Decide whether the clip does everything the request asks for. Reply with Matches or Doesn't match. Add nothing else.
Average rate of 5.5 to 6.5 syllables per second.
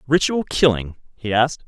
Doesn't match